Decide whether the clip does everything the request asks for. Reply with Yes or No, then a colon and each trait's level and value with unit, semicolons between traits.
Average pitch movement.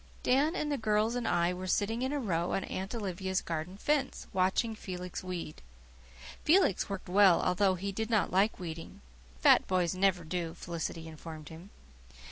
Yes: average, 3.9 semitones